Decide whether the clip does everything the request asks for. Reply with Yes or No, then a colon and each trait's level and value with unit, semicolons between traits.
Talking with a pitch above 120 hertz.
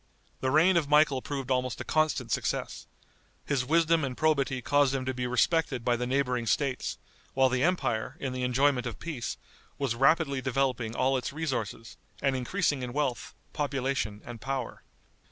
Yes: low, 135 Hz